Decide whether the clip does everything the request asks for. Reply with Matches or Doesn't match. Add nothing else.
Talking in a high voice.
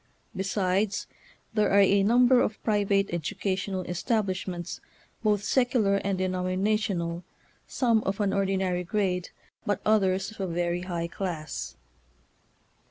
Matches